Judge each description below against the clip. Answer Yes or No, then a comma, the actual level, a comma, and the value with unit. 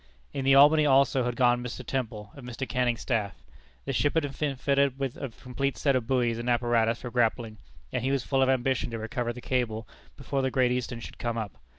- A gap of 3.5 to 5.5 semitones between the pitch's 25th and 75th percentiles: No, narrow, 2.4 semitones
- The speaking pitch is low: Yes, low, 125 Hz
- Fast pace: Yes, fast, 230 wpm